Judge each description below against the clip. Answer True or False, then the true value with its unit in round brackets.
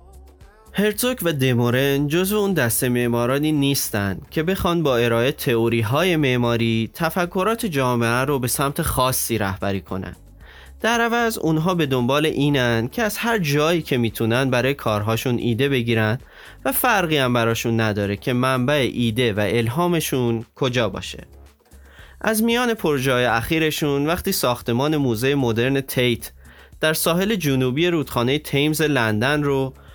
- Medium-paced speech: True (135 wpm)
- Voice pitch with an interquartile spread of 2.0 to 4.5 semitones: False (5.3 semitones)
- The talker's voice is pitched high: False (130 Hz)